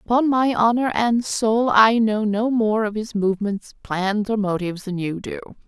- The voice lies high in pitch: Yes, high, 215 Hz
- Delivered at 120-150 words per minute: No, average, 190 wpm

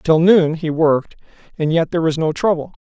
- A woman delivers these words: No, male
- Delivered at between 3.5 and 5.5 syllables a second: No, 5.7 syllables/s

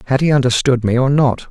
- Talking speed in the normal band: No, fast, 240 wpm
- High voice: No, low, 130 Hz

